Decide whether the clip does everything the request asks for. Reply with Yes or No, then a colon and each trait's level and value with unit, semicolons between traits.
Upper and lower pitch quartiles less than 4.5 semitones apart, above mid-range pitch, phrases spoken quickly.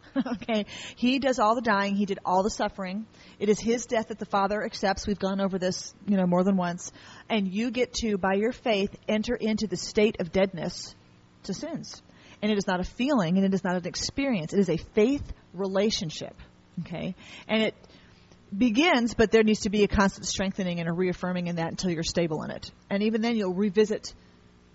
Yes: average, 3.3 semitones; high, 200 Hz; fast, 210 wpm